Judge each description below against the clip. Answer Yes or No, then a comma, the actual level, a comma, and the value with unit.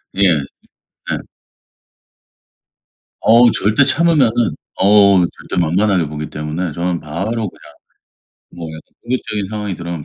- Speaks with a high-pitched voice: No, very low, 95 Hz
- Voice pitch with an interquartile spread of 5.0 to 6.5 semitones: No, average, 4.4 semitones